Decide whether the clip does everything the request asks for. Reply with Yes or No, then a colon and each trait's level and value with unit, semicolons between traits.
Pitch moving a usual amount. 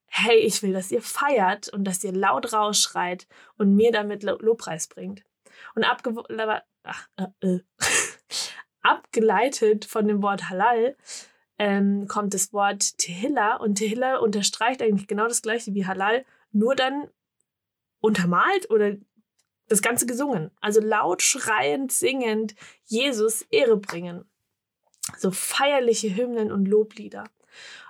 Yes: average, 3.0 semitones